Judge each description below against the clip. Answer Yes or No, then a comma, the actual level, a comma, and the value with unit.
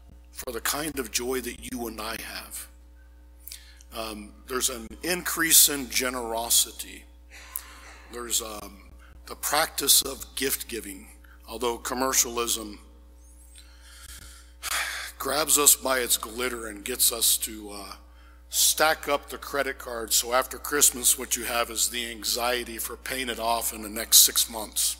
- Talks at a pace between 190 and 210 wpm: No, average, 140 wpm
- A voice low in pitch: Yes, low, 110 Hz